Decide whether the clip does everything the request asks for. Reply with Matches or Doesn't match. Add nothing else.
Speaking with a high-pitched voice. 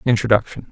Doesn't match